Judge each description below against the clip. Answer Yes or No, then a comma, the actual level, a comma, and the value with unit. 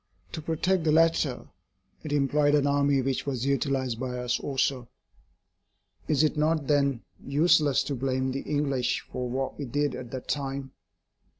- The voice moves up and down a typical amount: No, narrow, 2.2 semitones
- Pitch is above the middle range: No, medium, 140 Hz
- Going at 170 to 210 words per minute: No, average, 160 wpm